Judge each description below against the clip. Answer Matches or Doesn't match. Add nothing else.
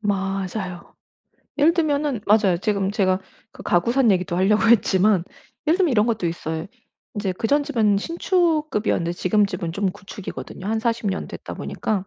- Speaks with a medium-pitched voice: Doesn't match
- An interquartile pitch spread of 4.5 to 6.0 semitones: Doesn't match